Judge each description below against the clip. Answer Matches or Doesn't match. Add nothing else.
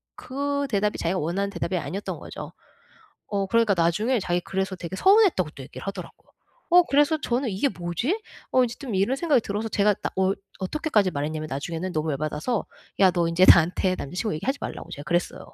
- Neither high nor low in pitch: Doesn't match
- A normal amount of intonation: Doesn't match